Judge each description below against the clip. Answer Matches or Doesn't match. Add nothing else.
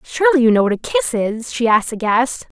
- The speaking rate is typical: Doesn't match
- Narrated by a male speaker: Doesn't match